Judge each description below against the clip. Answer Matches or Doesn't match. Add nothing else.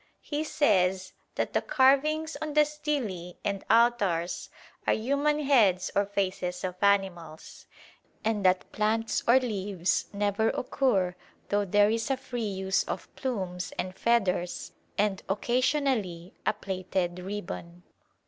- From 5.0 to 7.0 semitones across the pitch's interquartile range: Matches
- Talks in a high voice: Matches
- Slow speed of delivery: Matches